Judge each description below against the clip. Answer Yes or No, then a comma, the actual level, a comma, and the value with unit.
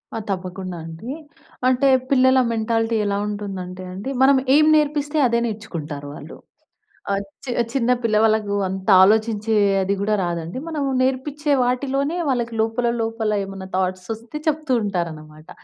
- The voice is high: Yes, high, 220 Hz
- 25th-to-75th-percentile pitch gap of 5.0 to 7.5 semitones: Yes, wide, 5.5 semitones